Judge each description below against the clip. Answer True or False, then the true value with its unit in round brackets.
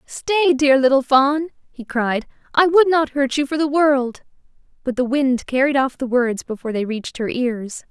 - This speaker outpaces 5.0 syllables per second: False (4.7 syllables/s)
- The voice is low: False (270 Hz)